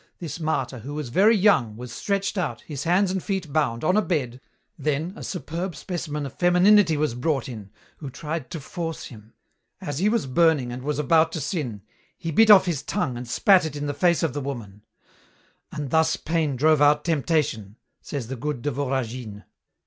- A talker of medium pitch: Yes, medium, 150 Hz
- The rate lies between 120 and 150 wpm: No, average, 195 wpm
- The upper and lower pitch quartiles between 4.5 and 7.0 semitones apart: Yes, average, 4.8 semitones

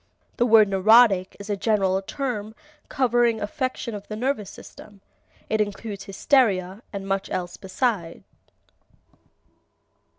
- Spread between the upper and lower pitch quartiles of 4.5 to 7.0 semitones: No, average, 3.0 semitones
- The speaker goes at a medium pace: No, slow, 120 wpm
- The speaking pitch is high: Yes, high, 210 Hz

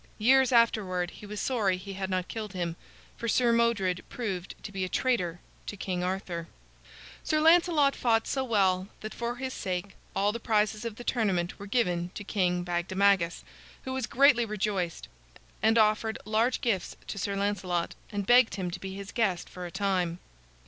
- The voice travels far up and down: No, average, 4.1 semitones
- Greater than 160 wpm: Yes, average, 180 wpm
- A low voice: No, high, 200 Hz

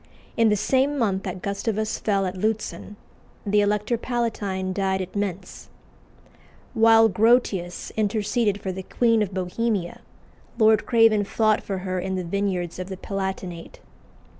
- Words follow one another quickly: No, average, 140 wpm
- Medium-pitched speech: No, high, 205 Hz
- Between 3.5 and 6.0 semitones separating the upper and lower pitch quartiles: No, average, 2.8 semitones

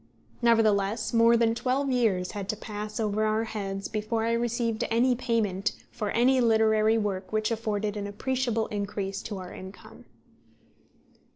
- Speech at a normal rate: Yes, average, 150 wpm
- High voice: Yes, high, 220 Hz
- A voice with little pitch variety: Yes, narrow, 2.2 semitones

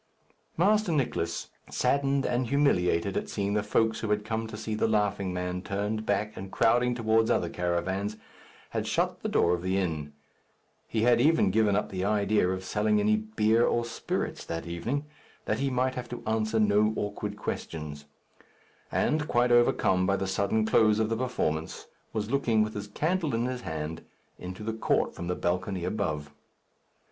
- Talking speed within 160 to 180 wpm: Yes, average, 175 wpm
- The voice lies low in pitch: Yes, low, 105 Hz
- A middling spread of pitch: Yes, average, 3.8 semitones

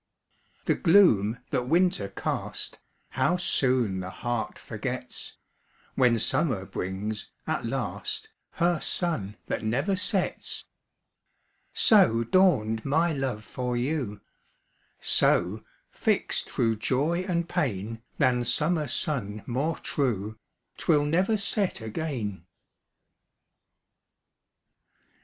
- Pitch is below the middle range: Yes, low, 125 Hz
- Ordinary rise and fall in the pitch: No, wide, 7.5 semitones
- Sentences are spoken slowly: Yes, slow, 95 wpm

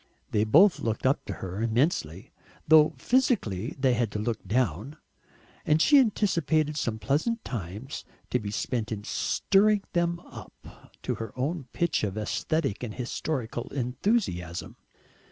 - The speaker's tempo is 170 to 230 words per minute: No, average, 140 wpm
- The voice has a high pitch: No, low, 130 Hz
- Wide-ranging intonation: Yes, wide, 7.1 semitones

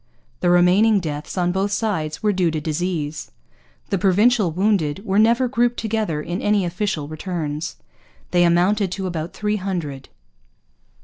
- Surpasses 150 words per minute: No, average, 145 wpm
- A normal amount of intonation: Yes, average, 4.4 semitones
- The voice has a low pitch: No, medium, 180 Hz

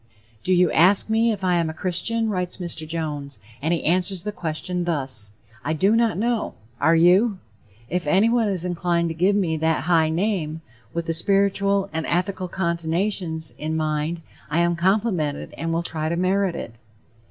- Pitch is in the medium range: Yes, medium, 175 Hz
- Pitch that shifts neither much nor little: Yes, average, 3.4 semitones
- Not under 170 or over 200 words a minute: Yes, average, 175 wpm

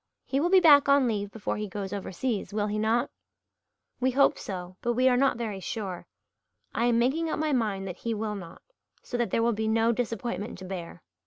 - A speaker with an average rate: No, fast, 220 wpm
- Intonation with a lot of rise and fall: No, average, 3.7 semitones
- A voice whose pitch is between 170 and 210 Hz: No, high, 225 Hz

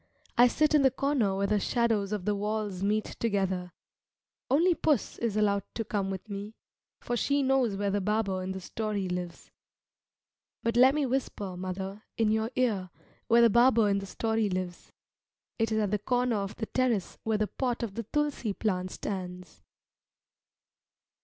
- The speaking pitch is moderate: No, high, 215 Hz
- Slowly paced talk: No, average, 175 wpm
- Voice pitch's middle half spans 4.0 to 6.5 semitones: No, average, 3.4 semitones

